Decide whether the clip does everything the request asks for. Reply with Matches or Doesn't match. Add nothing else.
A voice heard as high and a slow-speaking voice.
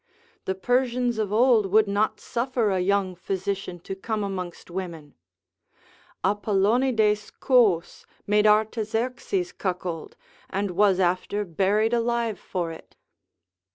Matches